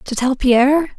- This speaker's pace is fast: No, average, 185 wpm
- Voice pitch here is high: Yes, very high, 265 Hz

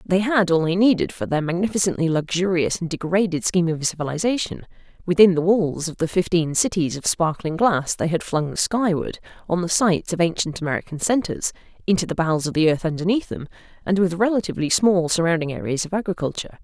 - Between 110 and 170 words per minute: No, average, 185 wpm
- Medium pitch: Yes, medium, 175 Hz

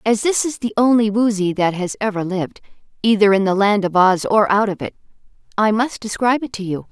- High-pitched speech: Yes, high, 210 Hz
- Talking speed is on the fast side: Yes, fast, 225 wpm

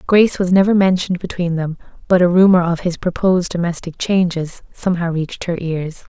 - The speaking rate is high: No, average, 175 wpm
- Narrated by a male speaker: No, female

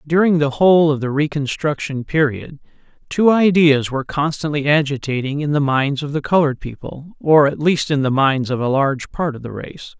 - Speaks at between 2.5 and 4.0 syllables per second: No, 5.3 syllables/s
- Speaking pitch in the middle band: Yes, medium, 145 Hz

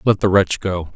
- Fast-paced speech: Yes, fast, 250 wpm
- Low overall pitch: Yes, very low, 95 Hz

